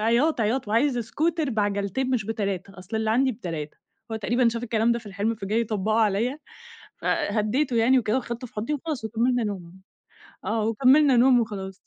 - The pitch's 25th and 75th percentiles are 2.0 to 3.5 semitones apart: Yes, average, 3.2 semitones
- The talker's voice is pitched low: No, high, 225 Hz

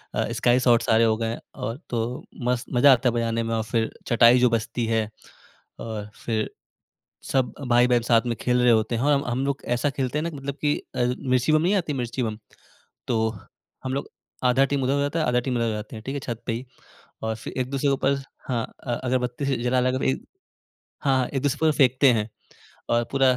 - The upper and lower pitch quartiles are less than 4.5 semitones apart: Yes, narrow, 2.6 semitones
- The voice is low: Yes, low, 125 Hz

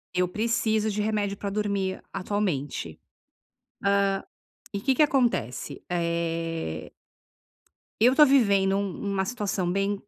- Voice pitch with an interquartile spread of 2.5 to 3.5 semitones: Yes, average, 3.2 semitones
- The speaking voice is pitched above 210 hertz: No, high, 200 Hz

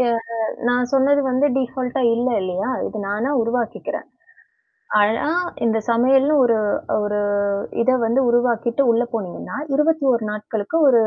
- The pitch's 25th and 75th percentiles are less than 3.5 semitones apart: Yes, average, 2.8 semitones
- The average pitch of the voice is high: Yes, high, 240 Hz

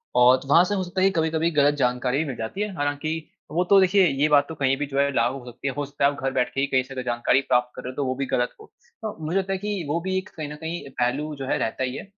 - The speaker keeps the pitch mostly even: No, average, 4.3 semitones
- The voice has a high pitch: No, medium, 145 Hz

